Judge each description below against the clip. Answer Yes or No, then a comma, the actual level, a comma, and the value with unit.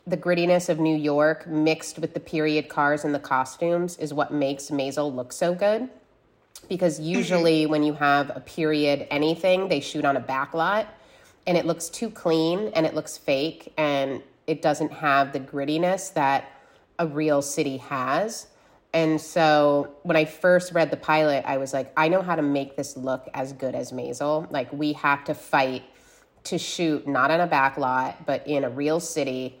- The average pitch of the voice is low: No, medium, 155 Hz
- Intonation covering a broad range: No, average, 2.7 semitones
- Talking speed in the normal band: Yes, average, 190 wpm